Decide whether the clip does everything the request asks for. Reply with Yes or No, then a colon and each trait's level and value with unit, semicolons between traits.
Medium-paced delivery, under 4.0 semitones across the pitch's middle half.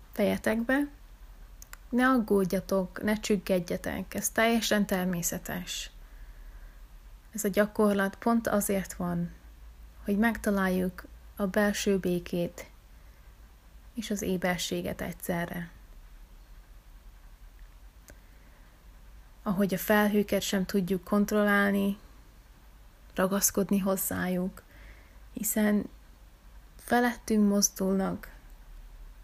No: slow, 70 wpm; narrow, 2.5 semitones